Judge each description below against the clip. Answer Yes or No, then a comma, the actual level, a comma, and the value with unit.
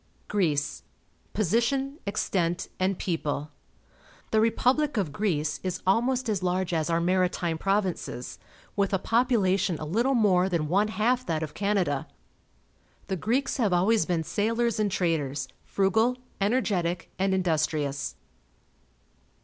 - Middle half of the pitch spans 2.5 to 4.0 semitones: No, average, 4.7 semitones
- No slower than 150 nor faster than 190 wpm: No, average, 140 wpm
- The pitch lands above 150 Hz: Yes, high, 190 Hz